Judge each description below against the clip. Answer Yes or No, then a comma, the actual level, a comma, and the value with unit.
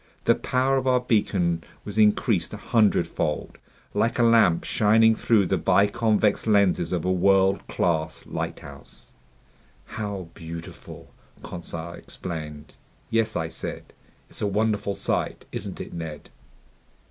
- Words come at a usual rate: No, slow, 125 wpm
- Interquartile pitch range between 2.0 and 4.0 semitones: No, average, 4.5 semitones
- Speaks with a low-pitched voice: Yes, low, 100 Hz